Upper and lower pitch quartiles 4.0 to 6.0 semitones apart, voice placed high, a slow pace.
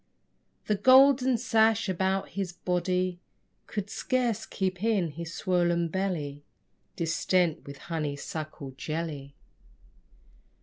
No: average, 4.3 semitones; medium, 180 Hz; slow, 100 wpm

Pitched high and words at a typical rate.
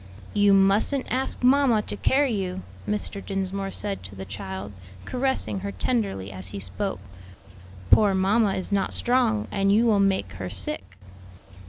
Yes: high, 195 Hz; average, 155 wpm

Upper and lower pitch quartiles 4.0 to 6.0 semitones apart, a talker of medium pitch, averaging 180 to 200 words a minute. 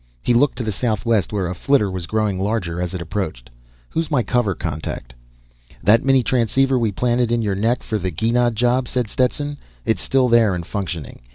No: average, 4.7 semitones; low, 110 Hz; average, 195 wpm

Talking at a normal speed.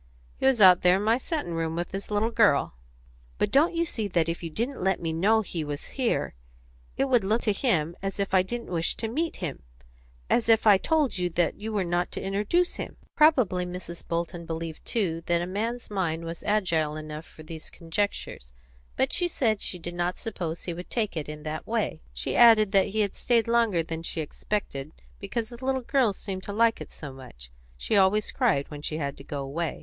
No: fast, 220 wpm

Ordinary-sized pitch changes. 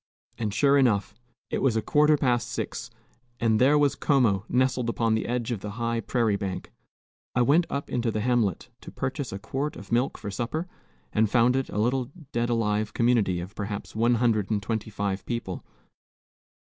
Yes: average, 3.1 semitones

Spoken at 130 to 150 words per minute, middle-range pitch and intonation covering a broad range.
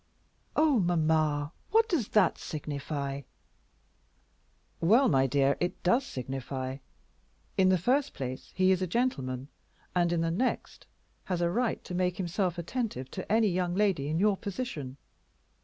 Yes: average, 145 wpm; medium, 175 Hz; wide, 6.2 semitones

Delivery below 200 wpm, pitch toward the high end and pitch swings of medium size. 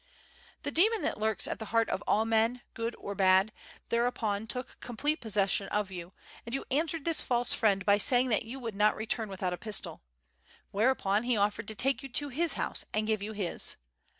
No: fast, 205 wpm; high, 220 Hz; average, 3.5 semitones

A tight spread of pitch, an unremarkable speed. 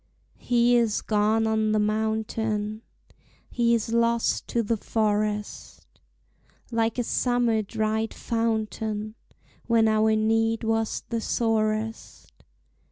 No: narrow, 1.1 semitones; slow, 105 wpm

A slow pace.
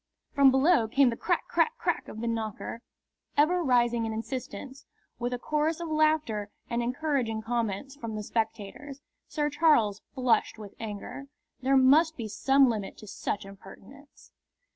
No: average, 155 wpm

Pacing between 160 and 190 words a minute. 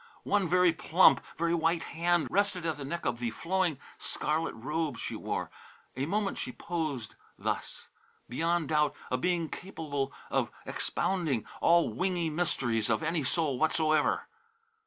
No: average, 145 wpm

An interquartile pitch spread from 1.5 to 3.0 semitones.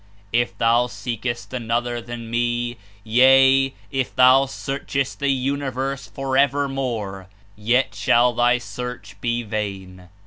Yes: narrow, 2.4 semitones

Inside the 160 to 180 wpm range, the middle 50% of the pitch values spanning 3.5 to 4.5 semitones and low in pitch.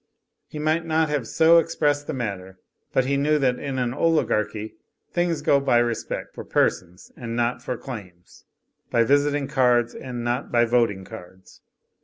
Yes: average, 165 wpm; average, 4.2 semitones; low, 125 Hz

